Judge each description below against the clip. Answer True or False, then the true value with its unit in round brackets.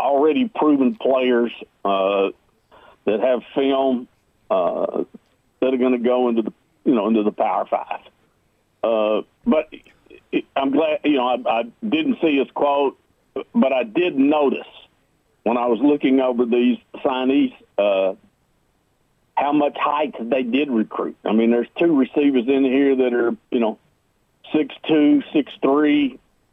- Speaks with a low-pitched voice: True (130 Hz)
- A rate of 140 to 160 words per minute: True (150 wpm)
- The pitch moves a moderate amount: True (3.5 semitones)